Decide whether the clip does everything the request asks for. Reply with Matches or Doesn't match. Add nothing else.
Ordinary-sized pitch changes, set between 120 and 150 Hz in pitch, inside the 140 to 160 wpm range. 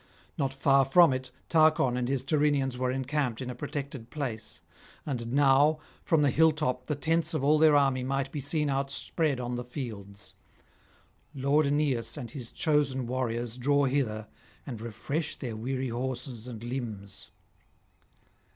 Matches